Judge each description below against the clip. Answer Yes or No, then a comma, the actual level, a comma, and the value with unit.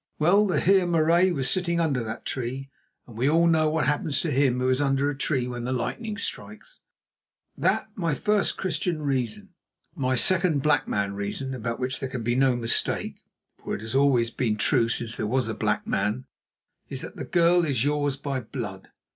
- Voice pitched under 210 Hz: Yes, low, 135 Hz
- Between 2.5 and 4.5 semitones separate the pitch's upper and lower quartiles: No, average, 4.9 semitones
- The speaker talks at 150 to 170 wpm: No, average, 200 wpm